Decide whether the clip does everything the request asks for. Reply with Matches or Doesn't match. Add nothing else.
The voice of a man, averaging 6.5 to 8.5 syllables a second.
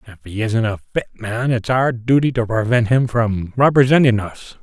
Doesn't match